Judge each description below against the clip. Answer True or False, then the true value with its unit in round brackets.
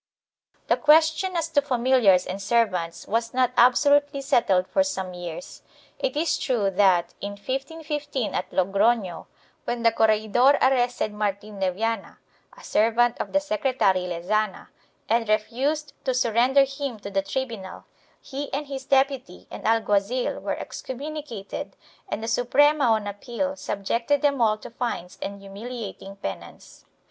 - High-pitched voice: True (235 Hz)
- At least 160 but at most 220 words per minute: False (145 wpm)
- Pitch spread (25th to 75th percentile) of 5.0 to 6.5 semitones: True (5.4 semitones)